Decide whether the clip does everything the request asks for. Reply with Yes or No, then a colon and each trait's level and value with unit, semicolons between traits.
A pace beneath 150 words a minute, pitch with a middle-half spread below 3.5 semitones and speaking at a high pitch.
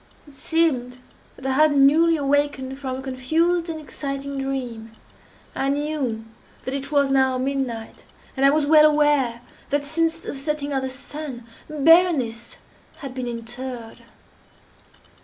Yes: average, 140 wpm; average, 2.7 semitones; very high, 275 Hz